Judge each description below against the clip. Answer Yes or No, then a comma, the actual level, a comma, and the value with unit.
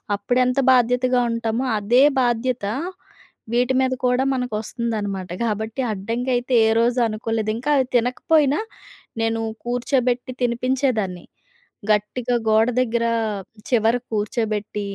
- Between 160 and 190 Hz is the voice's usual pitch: No, high, 235 Hz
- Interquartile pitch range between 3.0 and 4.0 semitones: No, narrow, 2.4 semitones